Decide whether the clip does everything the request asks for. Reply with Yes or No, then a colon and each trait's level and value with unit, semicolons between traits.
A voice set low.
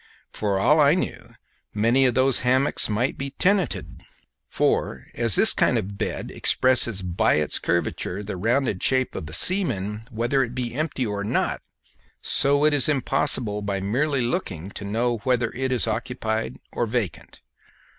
Yes: low, 120 Hz